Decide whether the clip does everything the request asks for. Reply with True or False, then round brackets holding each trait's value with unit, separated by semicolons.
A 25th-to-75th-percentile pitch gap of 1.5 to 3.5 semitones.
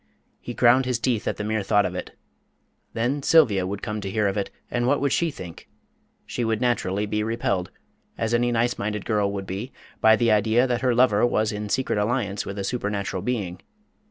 True (3.1 semitones)